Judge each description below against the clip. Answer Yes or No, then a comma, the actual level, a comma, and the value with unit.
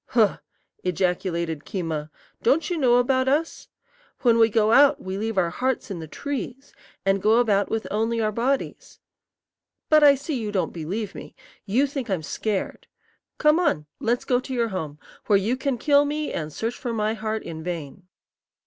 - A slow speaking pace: No, average, 180 wpm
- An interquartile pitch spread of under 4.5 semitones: No, wide, 5.6 semitones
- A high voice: Yes, high, 225 Hz